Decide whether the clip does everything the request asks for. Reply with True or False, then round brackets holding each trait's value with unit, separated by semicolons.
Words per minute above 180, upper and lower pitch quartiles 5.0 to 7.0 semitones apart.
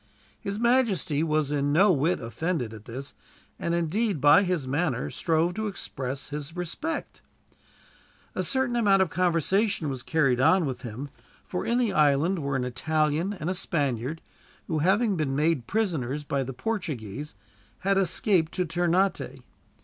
False (155 wpm; 5.4 semitones)